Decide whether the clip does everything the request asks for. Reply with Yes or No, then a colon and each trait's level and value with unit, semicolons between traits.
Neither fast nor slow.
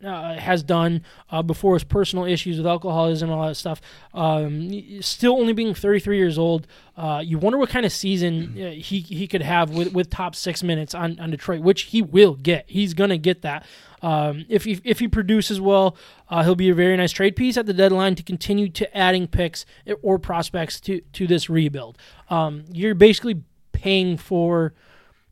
Yes: average, 195 wpm